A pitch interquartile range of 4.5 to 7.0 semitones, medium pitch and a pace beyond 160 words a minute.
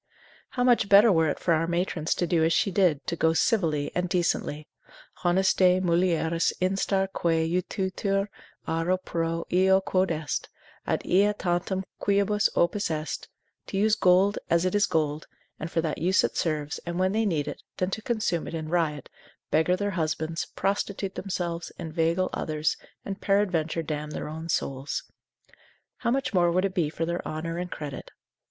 No: average, 3.0 semitones; medium, 175 Hz; average, 175 wpm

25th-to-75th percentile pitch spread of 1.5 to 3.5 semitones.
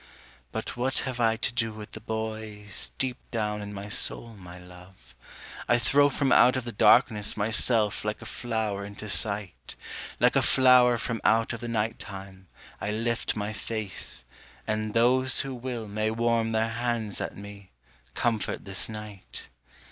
Yes: narrow, 2.5 semitones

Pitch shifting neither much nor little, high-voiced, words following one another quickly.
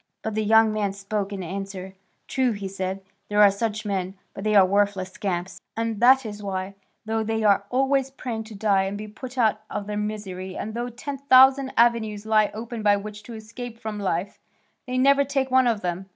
Yes: average, 3.0 semitones; high, 215 Hz; fast, 210 wpm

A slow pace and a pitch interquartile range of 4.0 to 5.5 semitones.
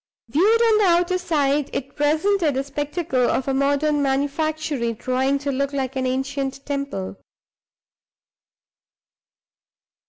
No: slow, 120 wpm; narrow, 2.5 semitones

